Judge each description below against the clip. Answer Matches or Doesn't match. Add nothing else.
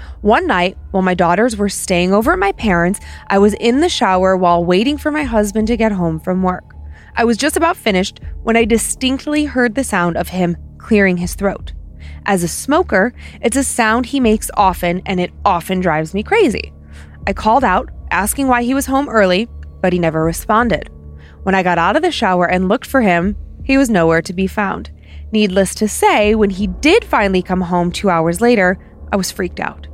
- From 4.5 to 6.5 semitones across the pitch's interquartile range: Matches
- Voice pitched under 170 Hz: Doesn't match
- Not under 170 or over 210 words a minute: Matches